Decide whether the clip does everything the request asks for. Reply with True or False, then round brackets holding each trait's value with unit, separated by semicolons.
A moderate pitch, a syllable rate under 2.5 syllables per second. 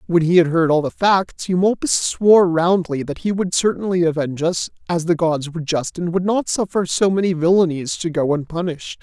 True (175 Hz; 2.0 syllables/s)